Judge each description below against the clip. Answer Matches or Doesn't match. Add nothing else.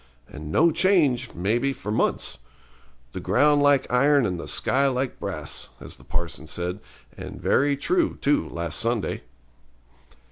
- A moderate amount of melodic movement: Doesn't match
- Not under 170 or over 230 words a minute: Doesn't match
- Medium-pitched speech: Doesn't match